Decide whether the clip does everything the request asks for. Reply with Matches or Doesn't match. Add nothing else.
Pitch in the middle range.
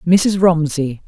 Matches